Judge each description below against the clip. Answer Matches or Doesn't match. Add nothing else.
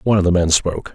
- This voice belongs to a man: Matches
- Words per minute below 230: Doesn't match